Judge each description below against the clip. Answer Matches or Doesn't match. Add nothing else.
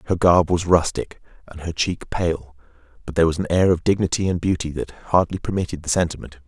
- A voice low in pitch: Matches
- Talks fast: Matches